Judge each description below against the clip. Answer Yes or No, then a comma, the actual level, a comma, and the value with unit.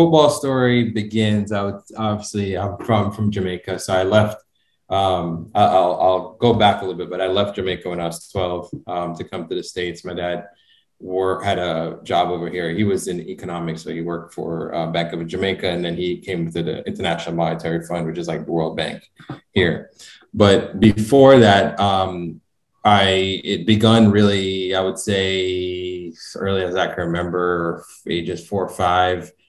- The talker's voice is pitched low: Yes, very low, 95 Hz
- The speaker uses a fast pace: No, average, 185 wpm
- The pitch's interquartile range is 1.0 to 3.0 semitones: Yes, average, 2.7 semitones